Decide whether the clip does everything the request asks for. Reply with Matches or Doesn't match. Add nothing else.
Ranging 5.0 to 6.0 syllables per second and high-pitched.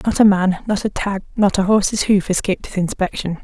Matches